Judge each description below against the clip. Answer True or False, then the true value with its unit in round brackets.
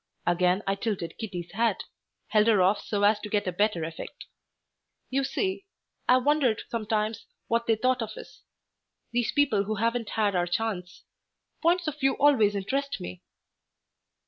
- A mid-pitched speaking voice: False (215 Hz)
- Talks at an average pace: True (160 wpm)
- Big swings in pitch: False (4.0 semitones)